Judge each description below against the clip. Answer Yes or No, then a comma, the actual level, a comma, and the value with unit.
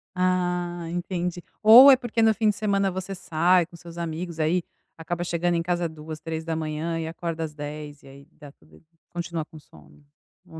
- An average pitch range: No, narrow, 2.2 semitones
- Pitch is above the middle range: No, medium, 170 Hz